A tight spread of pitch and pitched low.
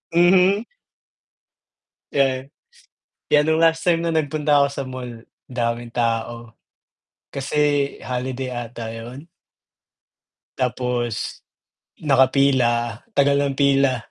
No: average, 3.5 semitones; low, 130 Hz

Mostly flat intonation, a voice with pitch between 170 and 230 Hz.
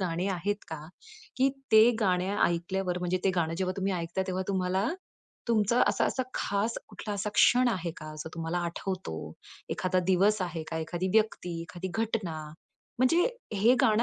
No: average, 3.5 semitones; high, 190 Hz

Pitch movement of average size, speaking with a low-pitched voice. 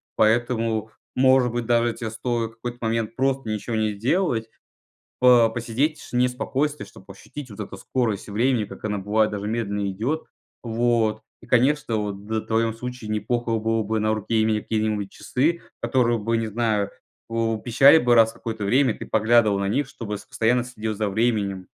No: narrow, 2.2 semitones; low, 115 Hz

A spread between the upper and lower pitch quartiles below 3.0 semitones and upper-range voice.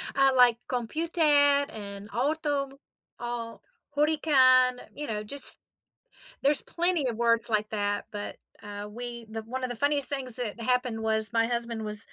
No: average, 3.6 semitones; high, 240 Hz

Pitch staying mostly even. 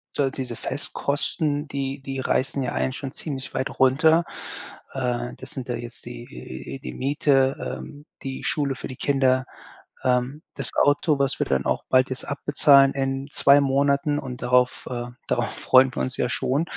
Yes: narrow, 1.7 semitones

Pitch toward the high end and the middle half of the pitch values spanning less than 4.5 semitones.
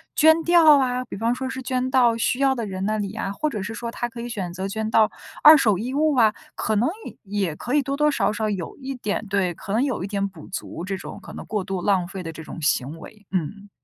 No: high, 215 Hz; average, 4.9 semitones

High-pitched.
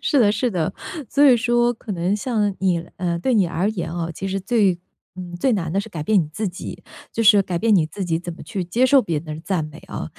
Yes: high, 195 Hz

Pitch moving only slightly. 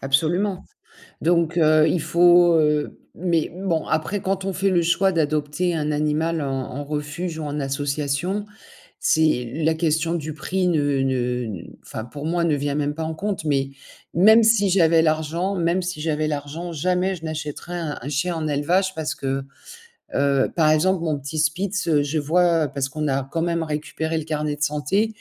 No: average, 3.0 semitones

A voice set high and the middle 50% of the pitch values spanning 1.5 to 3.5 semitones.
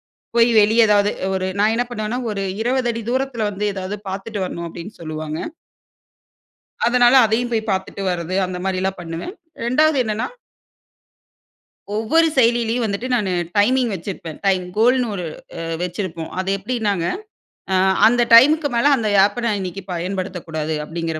No: high, 210 Hz; average, 4.5 semitones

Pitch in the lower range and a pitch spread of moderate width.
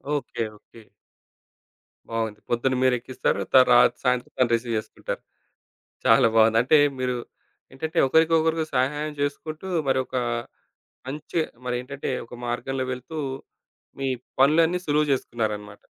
Yes: low, 130 Hz; average, 3.9 semitones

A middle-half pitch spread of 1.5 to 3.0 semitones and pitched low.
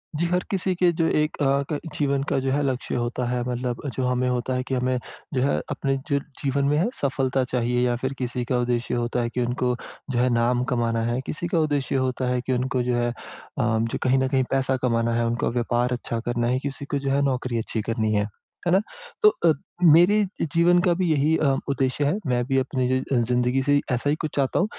Yes: narrow, 2.5 semitones; low, 130 Hz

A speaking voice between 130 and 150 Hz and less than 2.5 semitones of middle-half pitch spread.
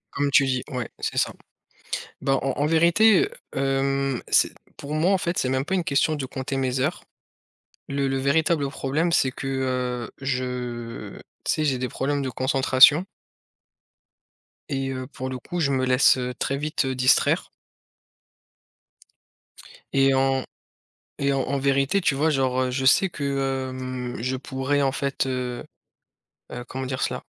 Yes: low, 135 Hz; narrow, 1.7 semitones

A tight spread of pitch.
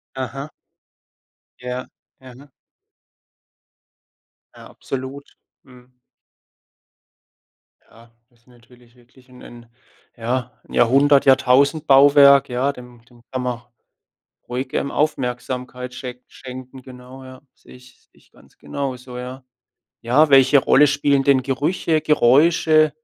Yes: narrow, 1.9 semitones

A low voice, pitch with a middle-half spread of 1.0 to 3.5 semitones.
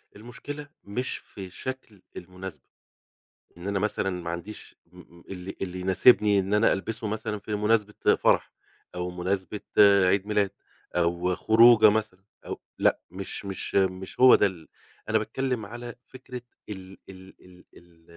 Yes: low, 100 Hz; average, 2.8 semitones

